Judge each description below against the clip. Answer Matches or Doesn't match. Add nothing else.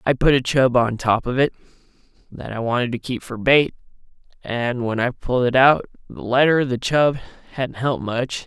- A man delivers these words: Matches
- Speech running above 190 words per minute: Doesn't match